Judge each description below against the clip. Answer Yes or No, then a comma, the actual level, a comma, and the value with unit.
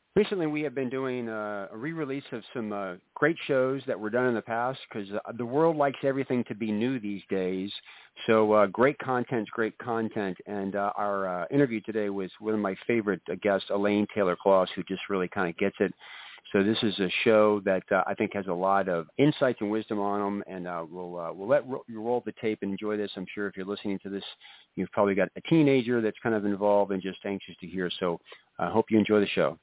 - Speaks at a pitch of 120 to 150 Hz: No, low, 105 Hz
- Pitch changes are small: No, average, 3.4 semitones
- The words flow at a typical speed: No, fast, 240 wpm